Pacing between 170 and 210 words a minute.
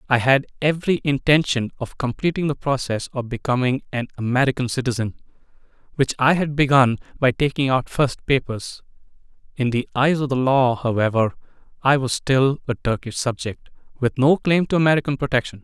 No: average, 155 wpm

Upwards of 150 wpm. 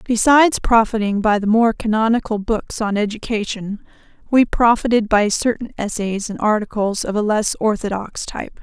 No: average, 145 wpm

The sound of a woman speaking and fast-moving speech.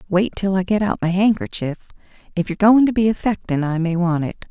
Yes: female; fast, 225 wpm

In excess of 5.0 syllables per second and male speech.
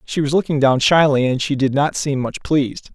Yes: 5.5 syllables/s; male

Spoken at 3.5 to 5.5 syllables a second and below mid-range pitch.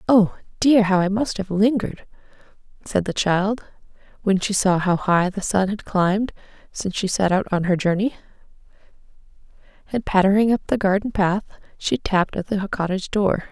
No: 5.3 syllables/s; high, 200 Hz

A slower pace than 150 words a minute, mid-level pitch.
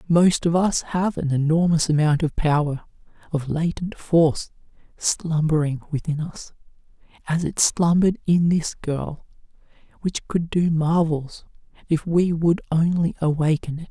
Yes: slow, 135 wpm; medium, 160 Hz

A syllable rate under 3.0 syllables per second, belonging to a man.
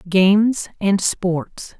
No: 2.7 syllables/s; female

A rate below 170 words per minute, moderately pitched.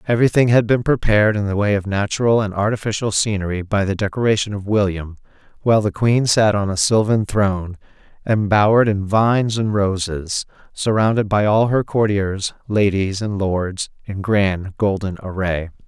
No: average, 160 wpm; low, 105 Hz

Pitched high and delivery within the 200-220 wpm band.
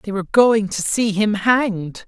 Yes: high, 210 Hz; fast, 205 wpm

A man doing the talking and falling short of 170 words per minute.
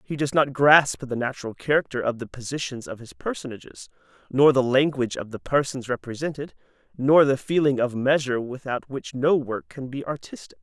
No: male; average, 180 wpm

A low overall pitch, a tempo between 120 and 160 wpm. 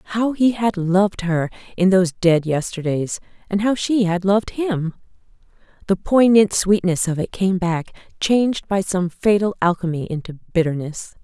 No: high, 190 Hz; average, 155 wpm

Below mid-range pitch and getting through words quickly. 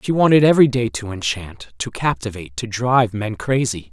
No: low, 115 Hz; average, 185 wpm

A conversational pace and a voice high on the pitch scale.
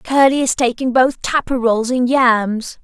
Yes: average, 170 wpm; very high, 250 Hz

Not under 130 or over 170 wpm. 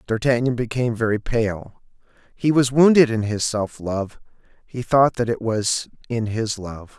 Yes: average, 165 wpm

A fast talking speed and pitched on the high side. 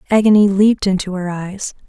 No: average, 160 wpm; high, 195 Hz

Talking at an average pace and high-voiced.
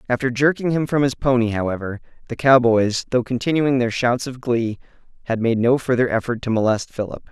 No: average, 190 wpm; low, 120 Hz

